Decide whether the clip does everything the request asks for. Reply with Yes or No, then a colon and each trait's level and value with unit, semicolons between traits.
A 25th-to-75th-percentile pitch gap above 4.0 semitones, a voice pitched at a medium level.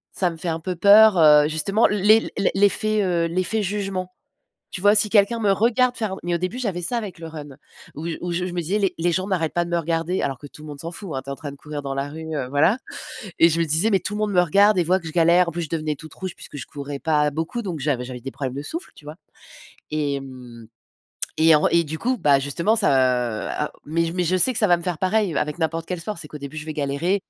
Yes: average, 4.4 semitones; medium, 170 Hz